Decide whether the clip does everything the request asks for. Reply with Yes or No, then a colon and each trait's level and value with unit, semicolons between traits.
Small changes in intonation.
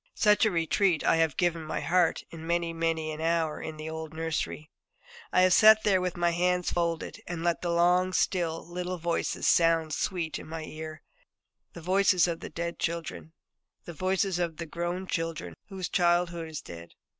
Yes: narrow, 1.8 semitones